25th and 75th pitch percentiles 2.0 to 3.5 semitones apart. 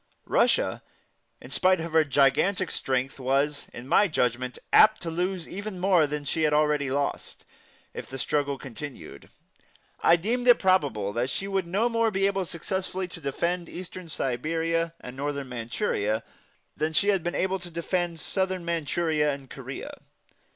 No: average, 5.0 semitones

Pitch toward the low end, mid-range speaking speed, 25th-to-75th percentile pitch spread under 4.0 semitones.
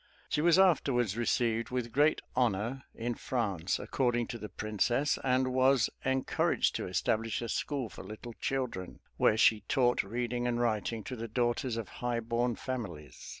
Yes: low, 120 Hz; average, 160 wpm; narrow, 2.4 semitones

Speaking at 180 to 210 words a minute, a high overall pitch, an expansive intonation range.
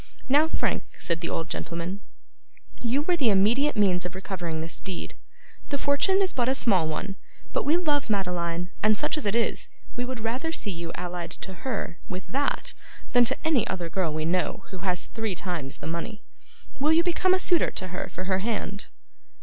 Yes: average, 200 wpm; high, 200 Hz; wide, 7.0 semitones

